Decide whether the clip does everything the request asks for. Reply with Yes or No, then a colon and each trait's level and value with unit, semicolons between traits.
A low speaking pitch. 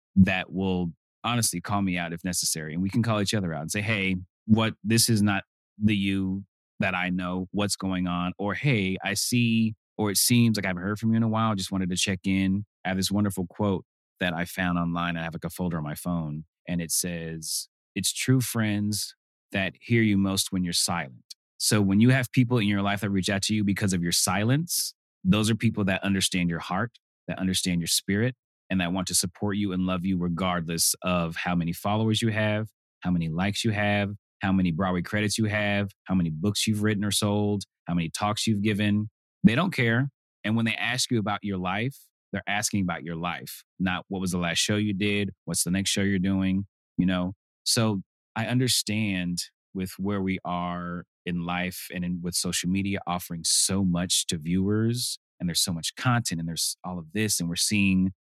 Yes: very low, 95 Hz